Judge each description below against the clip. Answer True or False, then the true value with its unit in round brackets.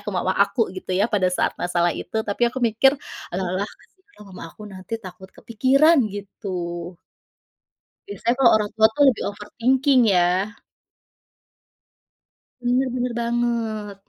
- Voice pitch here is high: True (210 Hz)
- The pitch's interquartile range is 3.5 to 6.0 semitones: True (4.4 semitones)